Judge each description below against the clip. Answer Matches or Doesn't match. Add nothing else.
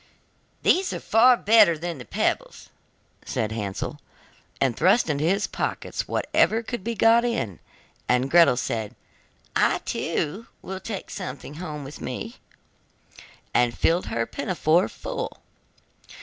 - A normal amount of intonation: Doesn't match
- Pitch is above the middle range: Doesn't match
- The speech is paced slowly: Matches